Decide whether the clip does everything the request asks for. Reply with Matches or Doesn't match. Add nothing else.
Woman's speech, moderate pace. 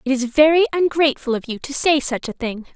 Doesn't match